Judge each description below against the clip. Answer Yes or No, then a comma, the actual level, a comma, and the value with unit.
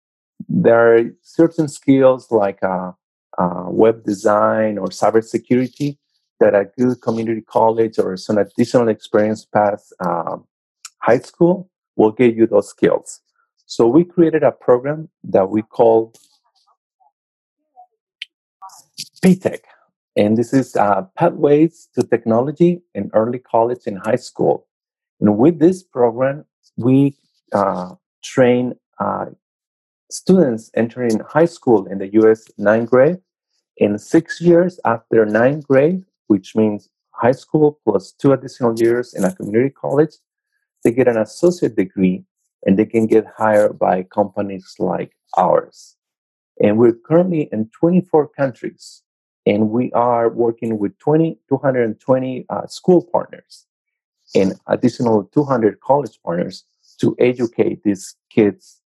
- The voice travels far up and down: Yes, wide, 6.9 semitones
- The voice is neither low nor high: No, low, 120 Hz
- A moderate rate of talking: No, slow, 125 wpm